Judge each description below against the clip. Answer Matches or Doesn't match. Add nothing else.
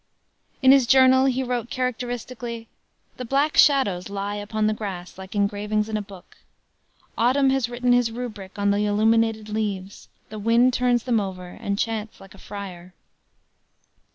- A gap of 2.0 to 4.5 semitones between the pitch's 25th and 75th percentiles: Matches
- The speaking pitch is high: Matches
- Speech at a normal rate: Matches